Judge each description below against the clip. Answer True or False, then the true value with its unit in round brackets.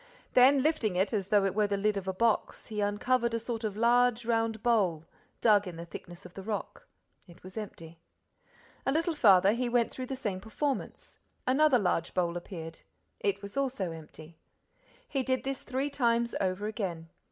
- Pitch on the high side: True (215 Hz)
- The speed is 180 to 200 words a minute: True (185 wpm)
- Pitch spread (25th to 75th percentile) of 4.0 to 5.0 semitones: True (4.7 semitones)